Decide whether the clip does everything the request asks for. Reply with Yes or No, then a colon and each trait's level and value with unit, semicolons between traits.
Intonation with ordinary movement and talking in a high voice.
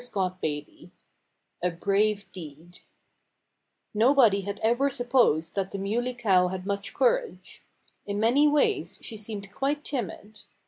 Yes: average, 4.6 semitones; high, 205 Hz